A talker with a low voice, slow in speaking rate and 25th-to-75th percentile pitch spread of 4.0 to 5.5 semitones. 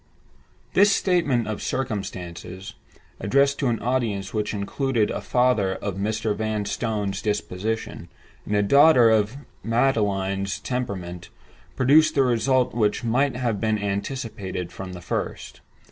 Yes: low, 110 Hz; slow, 115 wpm; average, 4.3 semitones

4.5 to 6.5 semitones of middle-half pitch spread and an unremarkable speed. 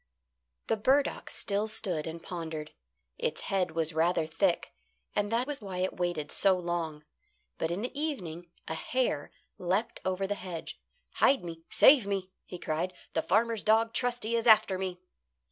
Yes: average, 4.8 semitones; average, 160 wpm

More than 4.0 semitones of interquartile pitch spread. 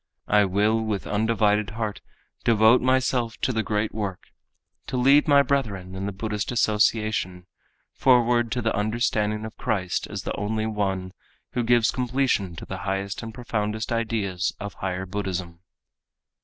No: average, 2.9 semitones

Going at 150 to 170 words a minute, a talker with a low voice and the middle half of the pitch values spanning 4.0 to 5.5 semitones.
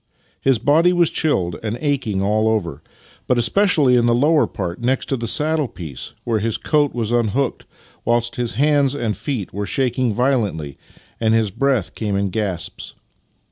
Yes: average, 165 wpm; low, 120 Hz; average, 5.0 semitones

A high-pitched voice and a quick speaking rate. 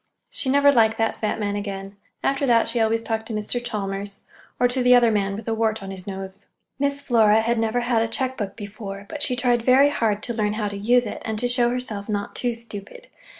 Yes: high, 225 Hz; fast, 235 wpm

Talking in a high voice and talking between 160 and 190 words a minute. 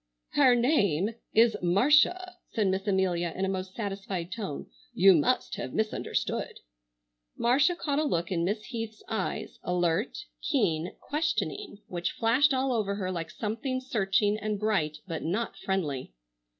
No: high, 205 Hz; average, 145 wpm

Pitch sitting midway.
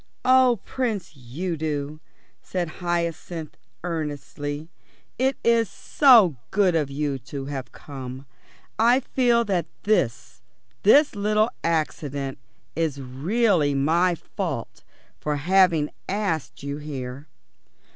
Yes: medium, 165 Hz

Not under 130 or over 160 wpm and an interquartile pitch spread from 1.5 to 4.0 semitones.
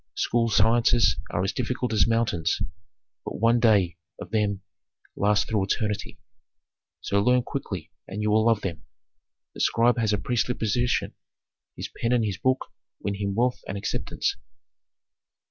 Yes: average, 150 wpm; average, 2.8 semitones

